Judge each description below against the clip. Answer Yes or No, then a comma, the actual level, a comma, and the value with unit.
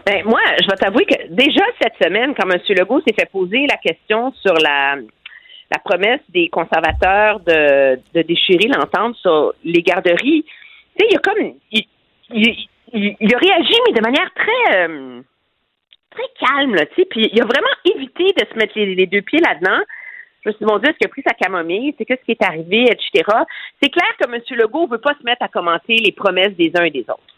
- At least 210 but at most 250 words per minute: Yes, average, 215 wpm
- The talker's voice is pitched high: Yes, high, 235 Hz